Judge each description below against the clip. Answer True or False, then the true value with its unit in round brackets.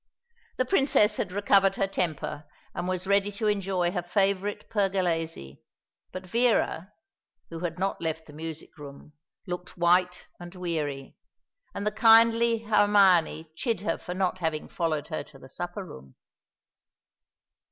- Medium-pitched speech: True (180 Hz)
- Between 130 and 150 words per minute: True (140 wpm)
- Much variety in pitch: False (3.7 semitones)